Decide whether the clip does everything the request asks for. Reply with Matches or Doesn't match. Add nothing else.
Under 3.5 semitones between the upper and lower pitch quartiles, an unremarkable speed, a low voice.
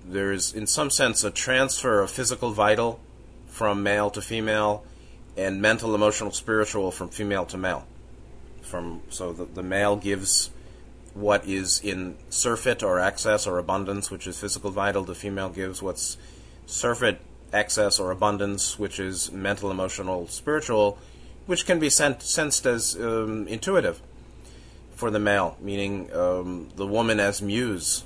Matches